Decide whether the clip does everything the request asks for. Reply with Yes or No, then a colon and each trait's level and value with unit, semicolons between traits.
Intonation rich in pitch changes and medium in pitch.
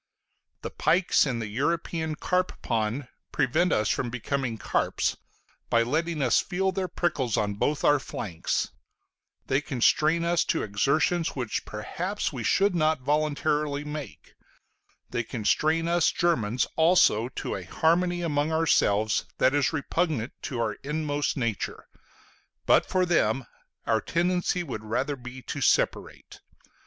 Yes: wide, 6.0 semitones; medium, 145 Hz